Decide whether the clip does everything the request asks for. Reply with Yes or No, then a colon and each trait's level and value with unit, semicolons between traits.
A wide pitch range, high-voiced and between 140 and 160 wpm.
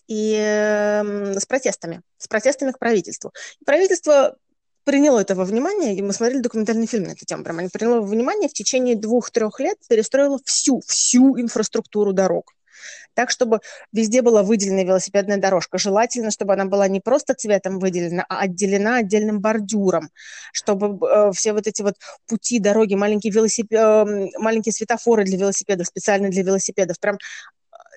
No: average, 3.2 semitones; high, 215 Hz; average, 155 wpm